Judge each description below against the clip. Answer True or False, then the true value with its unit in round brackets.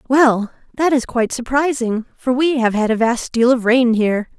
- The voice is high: True (245 Hz)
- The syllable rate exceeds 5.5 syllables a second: False (4.9 syllables/s)